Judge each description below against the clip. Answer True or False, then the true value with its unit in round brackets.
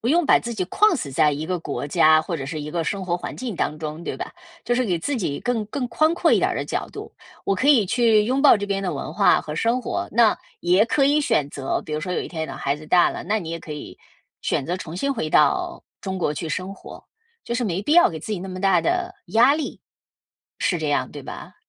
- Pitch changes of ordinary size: False (7.1 semitones)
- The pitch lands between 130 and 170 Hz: False (185 Hz)